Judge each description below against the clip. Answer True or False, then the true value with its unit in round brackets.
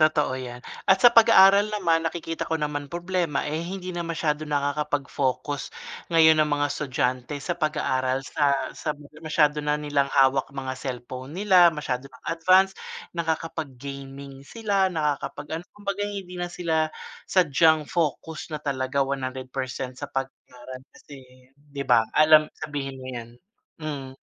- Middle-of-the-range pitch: True (150 Hz)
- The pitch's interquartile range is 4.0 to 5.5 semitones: False (3.5 semitones)